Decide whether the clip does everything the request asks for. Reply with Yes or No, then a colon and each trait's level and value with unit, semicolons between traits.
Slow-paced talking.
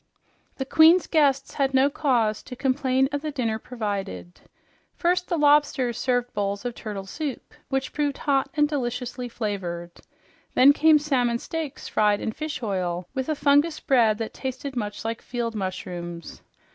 No: average, 160 wpm